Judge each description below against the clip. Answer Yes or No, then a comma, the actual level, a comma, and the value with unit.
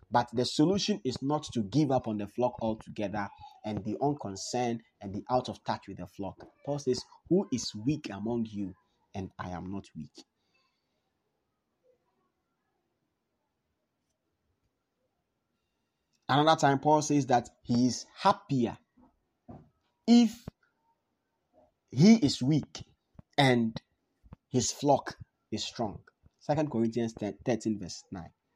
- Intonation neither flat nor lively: No, wide, 5.7 semitones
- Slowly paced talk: Yes, slow, 120 wpm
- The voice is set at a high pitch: No, low, 125 Hz